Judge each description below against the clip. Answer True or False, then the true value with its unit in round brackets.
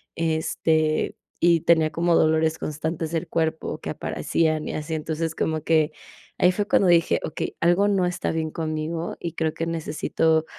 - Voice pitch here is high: False (160 Hz)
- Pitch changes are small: True (1.1 semitones)